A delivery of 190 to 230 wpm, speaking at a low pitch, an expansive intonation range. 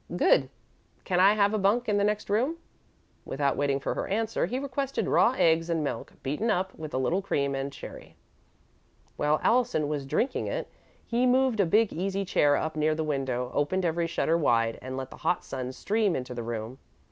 No: average, 200 wpm; medium, 165 Hz; wide, 7.2 semitones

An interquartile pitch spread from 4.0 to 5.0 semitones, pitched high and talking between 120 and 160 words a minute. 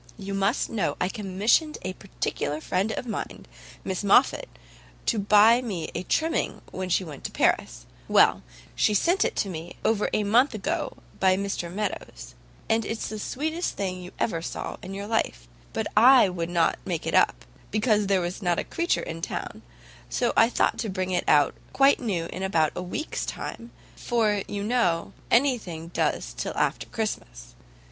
No: average, 4.3 semitones; high, 200 Hz; average, 180 wpm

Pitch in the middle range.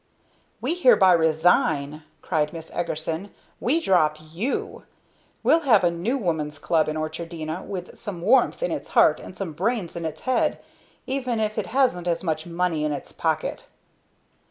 Yes: medium, 170 Hz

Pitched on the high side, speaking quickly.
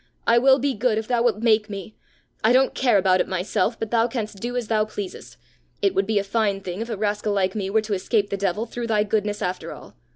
Yes: high, 215 Hz; fast, 255 wpm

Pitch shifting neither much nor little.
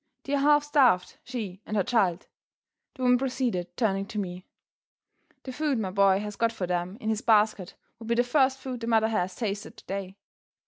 Yes: average, 4.4 semitones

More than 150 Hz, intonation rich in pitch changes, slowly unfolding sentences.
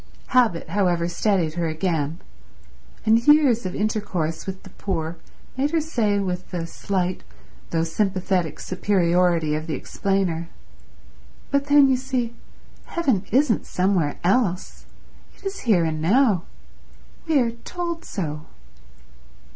Yes: high, 190 Hz; wide, 6.0 semitones; slow, 125 wpm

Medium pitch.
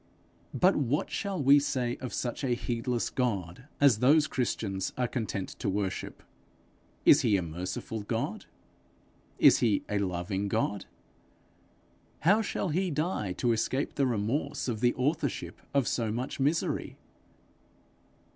No: low, 120 Hz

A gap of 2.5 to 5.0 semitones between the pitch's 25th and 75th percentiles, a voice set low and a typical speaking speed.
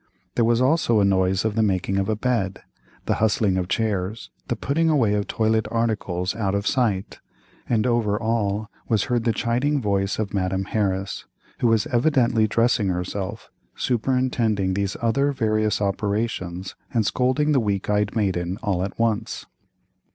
Yes: average, 3.1 semitones; low, 110 Hz; average, 160 wpm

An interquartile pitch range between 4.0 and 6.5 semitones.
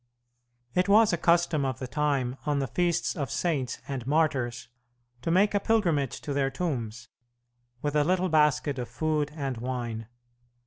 Yes: average, 4.6 semitones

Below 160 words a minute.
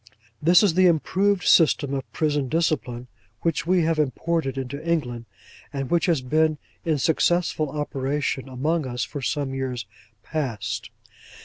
Yes: average, 140 wpm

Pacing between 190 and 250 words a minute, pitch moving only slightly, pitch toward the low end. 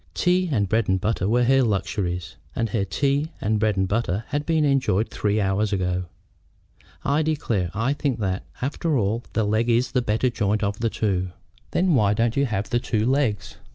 No: average, 195 wpm; average, 4.9 semitones; low, 110 Hz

